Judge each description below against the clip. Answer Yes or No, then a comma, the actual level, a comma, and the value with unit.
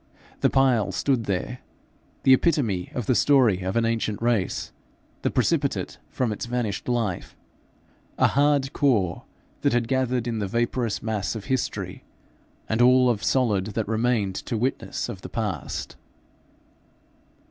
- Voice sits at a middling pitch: No, low, 120 Hz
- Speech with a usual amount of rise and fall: Yes, average, 3.2 semitones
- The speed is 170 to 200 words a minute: No, average, 145 wpm